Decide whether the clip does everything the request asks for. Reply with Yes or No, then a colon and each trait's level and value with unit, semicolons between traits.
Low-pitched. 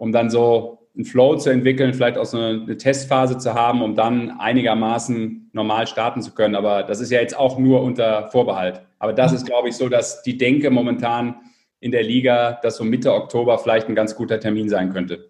Yes: low, 120 Hz